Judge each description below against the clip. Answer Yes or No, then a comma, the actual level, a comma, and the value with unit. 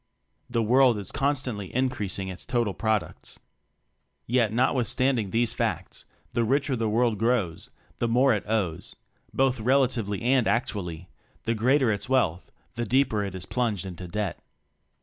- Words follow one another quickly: No, average, 145 wpm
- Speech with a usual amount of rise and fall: Yes, average, 3.9 semitones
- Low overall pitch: Yes, low, 115 Hz